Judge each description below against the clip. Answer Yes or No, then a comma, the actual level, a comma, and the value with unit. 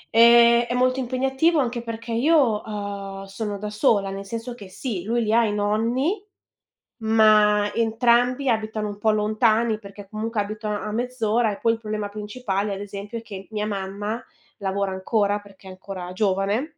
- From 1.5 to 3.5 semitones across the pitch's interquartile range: Yes, narrow, 2.5 semitones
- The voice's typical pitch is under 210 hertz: No, high, 215 Hz